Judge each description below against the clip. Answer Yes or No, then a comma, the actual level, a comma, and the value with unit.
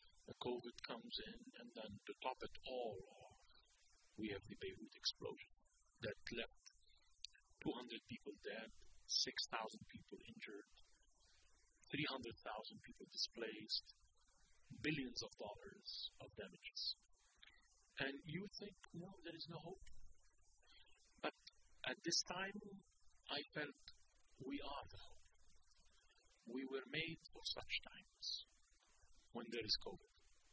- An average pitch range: No, wide, 7.1 semitones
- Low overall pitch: No, medium, 165 Hz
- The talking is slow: Yes, slow, 125 wpm